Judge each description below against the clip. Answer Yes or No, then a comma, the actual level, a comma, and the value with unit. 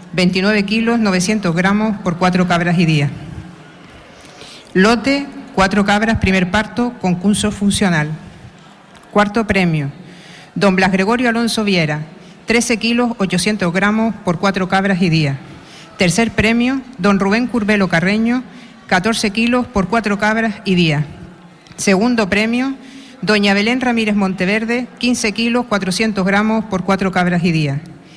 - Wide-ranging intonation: No, average, 3.8 semitones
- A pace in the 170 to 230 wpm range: No, average, 130 wpm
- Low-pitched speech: No, high, 200 Hz